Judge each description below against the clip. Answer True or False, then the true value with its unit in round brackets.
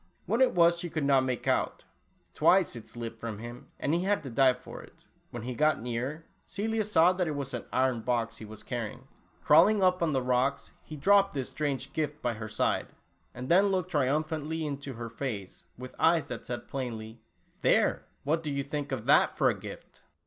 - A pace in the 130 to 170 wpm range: False (205 wpm)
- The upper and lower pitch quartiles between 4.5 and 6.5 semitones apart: True (5.0 semitones)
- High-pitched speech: False (140 Hz)